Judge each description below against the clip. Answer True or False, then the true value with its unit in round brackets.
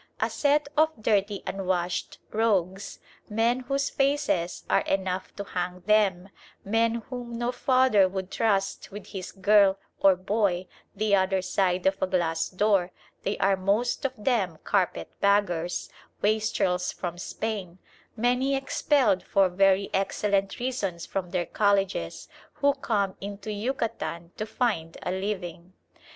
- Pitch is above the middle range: True (200 Hz)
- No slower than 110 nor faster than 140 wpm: True (135 wpm)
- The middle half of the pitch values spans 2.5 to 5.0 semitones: True (3.3 semitones)